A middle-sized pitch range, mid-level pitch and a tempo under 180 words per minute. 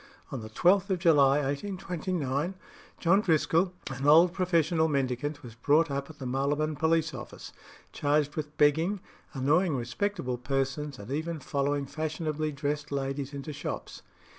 Yes: average, 3.1 semitones; medium, 150 Hz; average, 140 wpm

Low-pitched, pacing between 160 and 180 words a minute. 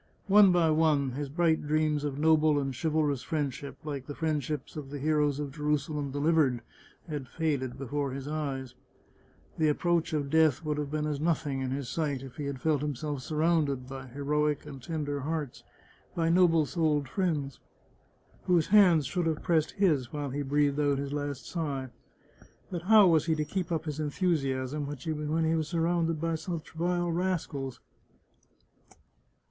No: medium, 150 Hz; average, 170 wpm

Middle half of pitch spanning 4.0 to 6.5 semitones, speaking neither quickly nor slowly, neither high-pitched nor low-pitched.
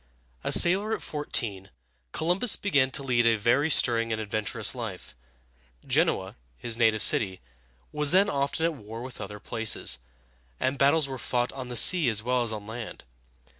No: average, 4.6 semitones; average, 170 wpm; low, 120 Hz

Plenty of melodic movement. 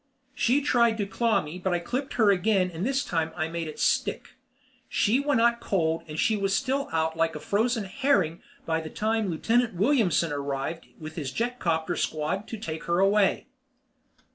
Yes: wide, 6.2 semitones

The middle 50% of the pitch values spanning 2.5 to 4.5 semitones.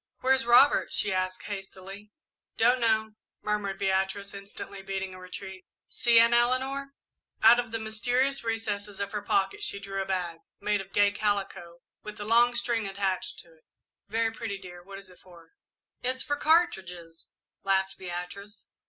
Yes: average, 3.1 semitones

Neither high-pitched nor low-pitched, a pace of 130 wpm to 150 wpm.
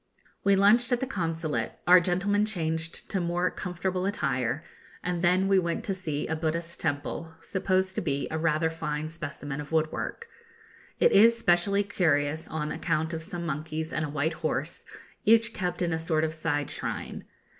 No: medium, 170 Hz; average, 175 wpm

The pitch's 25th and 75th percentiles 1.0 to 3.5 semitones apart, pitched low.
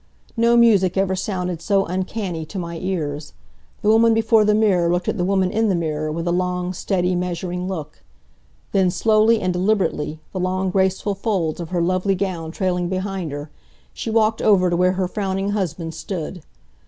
No: narrow, 2.4 semitones; medium, 185 Hz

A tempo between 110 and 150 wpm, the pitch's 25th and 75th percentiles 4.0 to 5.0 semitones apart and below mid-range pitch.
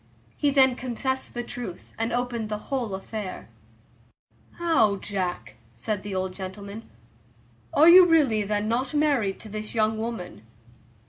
No: average, 145 wpm; average, 4.4 semitones; high, 220 Hz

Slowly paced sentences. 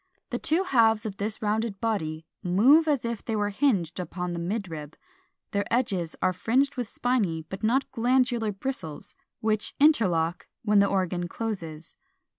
No: average, 155 wpm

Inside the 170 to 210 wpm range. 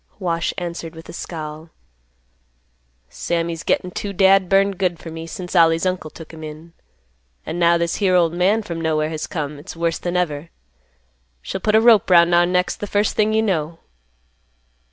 Yes: average, 180 wpm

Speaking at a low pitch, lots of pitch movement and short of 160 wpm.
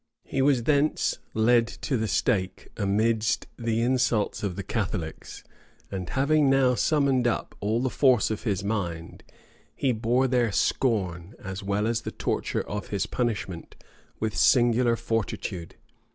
No: low, 115 Hz; average, 3.8 semitones; average, 145 wpm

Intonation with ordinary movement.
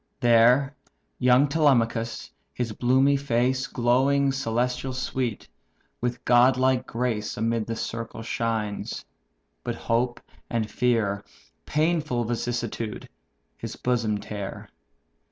No: narrow, 2.3 semitones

